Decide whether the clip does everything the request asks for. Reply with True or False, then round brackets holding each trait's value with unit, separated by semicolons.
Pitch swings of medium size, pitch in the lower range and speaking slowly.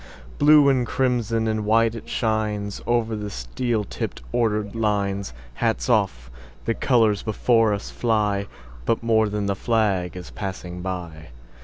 True (3.6 semitones; 105 Hz; 125 wpm)